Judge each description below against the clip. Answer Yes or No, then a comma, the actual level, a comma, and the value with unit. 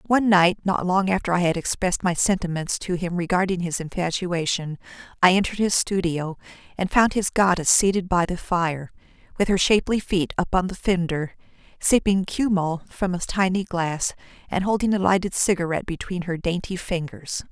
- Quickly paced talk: No, average, 170 wpm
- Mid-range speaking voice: Yes, medium, 180 Hz